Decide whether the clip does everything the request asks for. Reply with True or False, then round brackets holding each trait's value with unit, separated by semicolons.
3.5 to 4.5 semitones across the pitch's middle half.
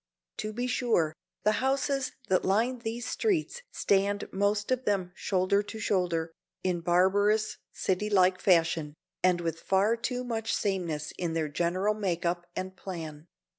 True (3.8 semitones)